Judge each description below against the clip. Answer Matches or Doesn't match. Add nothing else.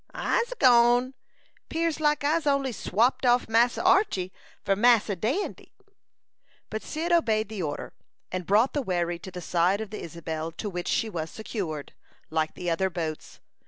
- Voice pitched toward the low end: Doesn't match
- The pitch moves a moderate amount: Doesn't match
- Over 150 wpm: Matches